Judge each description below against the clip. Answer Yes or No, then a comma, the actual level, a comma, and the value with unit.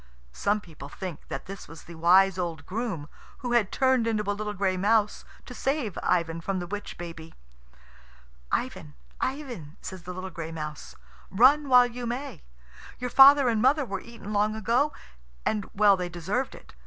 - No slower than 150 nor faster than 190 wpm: Yes, average, 175 wpm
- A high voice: Yes, high, 205 Hz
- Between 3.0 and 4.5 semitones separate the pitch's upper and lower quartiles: No, wide, 5.6 semitones